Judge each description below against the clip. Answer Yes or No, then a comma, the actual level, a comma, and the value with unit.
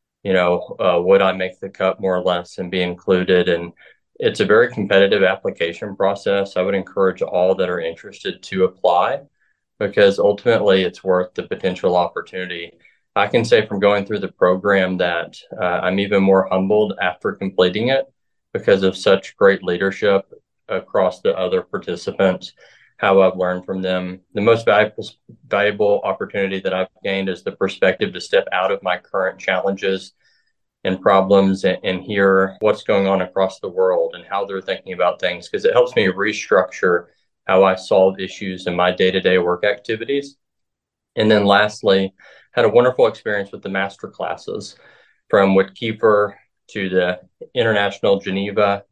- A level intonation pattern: No, average, 4.4 semitones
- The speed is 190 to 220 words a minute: No, average, 165 wpm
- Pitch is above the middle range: No, very low, 95 Hz